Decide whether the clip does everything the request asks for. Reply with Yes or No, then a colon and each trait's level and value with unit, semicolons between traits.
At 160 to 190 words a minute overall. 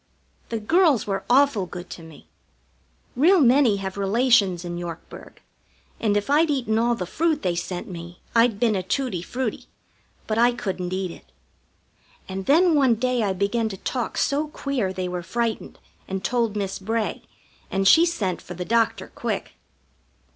Yes: average, 170 wpm